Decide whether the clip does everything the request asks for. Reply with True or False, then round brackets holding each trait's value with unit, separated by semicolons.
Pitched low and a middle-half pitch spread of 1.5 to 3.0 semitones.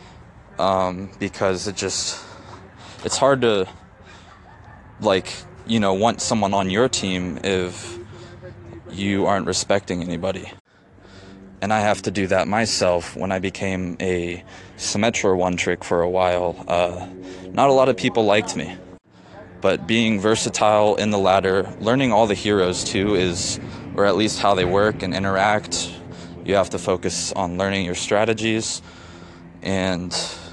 True (95 Hz; 2.5 semitones)